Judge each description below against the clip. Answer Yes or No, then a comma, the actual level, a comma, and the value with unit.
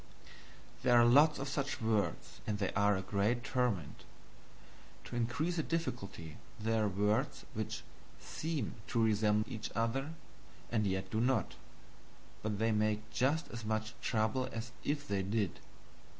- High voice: No, low, 110 Hz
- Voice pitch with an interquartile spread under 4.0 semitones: Yes, average, 3.6 semitones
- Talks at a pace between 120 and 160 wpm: Yes, average, 150 wpm